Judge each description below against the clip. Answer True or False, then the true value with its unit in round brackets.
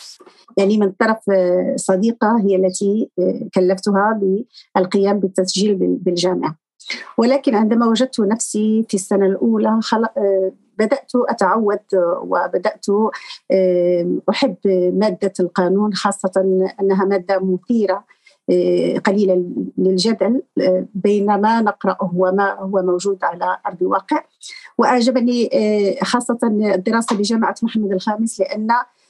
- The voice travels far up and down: False (3.1 semitones)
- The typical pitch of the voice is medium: False (205 Hz)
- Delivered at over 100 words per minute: False (95 wpm)